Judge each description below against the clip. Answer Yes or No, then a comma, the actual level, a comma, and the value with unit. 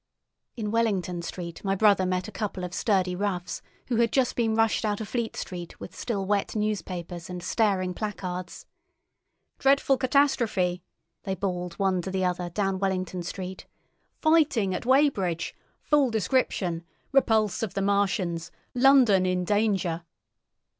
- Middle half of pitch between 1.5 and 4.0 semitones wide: Yes, average, 3.7 semitones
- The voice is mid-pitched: No, high, 195 Hz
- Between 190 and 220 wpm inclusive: No, average, 145 wpm